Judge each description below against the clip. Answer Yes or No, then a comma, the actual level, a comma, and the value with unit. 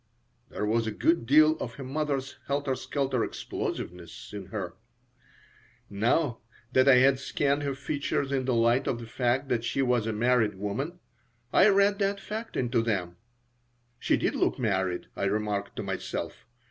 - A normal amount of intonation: Yes, average, 4.6 semitones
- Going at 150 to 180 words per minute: Yes, average, 165 wpm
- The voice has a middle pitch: No, low, 125 Hz